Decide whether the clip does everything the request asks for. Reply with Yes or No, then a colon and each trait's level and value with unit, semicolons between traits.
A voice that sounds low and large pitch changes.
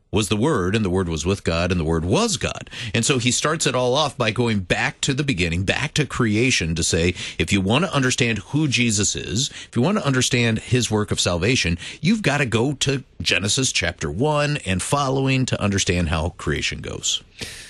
Yes: low, 115 Hz; wide, 5.9 semitones